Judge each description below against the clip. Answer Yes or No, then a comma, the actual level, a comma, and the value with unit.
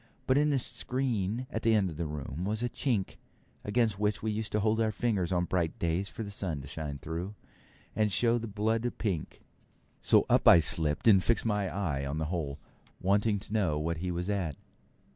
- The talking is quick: Yes, fast, 210 wpm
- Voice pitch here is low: Yes, low, 100 Hz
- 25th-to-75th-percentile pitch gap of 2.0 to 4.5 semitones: No, average, 4.9 semitones